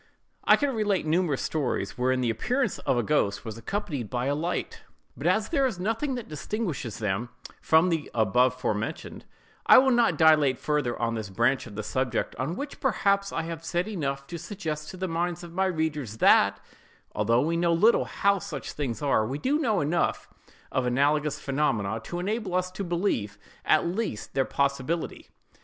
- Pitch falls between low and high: Yes, medium, 155 Hz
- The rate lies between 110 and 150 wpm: No, average, 185 wpm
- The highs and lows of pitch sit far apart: Yes, wide, 6.7 semitones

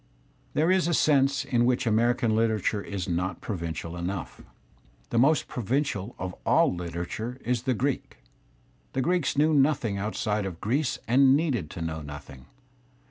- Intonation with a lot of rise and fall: Yes, wide, 6.7 semitones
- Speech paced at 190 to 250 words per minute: No, average, 150 wpm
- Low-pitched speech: Yes, low, 115 Hz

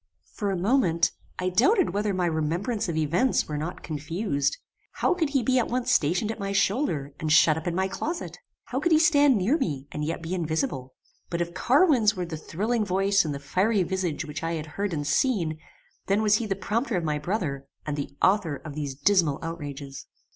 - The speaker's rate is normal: No, fast, 210 wpm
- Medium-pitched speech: Yes, medium, 180 Hz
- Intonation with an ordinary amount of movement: No, wide, 5.9 semitones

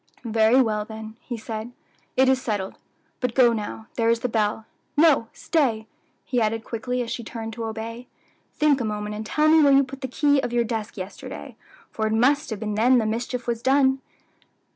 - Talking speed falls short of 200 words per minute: No, fast, 205 wpm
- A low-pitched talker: No, high, 230 Hz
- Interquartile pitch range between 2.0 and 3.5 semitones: Yes, average, 3.0 semitones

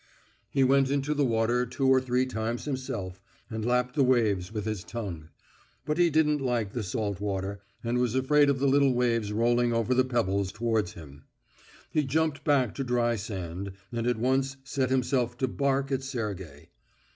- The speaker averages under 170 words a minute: No, average, 180 wpm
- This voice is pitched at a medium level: No, low, 120 Hz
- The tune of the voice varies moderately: Yes, average, 3.7 semitones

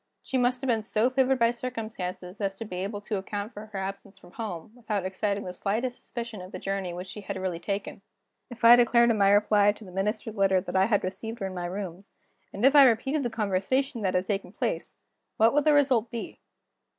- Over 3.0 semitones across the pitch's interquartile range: Yes, average, 3.5 semitones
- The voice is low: No, high, 210 Hz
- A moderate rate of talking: No, fast, 230 wpm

